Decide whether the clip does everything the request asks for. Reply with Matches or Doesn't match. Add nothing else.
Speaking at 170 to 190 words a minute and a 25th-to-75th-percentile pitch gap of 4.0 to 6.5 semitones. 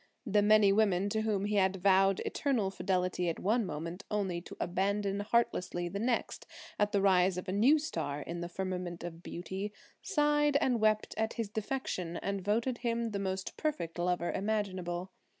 Doesn't match